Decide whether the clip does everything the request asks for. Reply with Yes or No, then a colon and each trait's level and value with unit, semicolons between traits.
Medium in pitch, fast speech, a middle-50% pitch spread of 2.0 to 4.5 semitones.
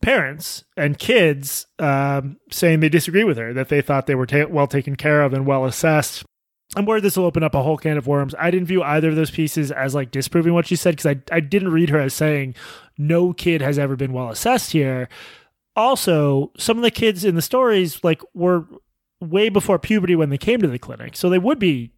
Yes: medium, 155 Hz; fast, 230 wpm; average, 4.2 semitones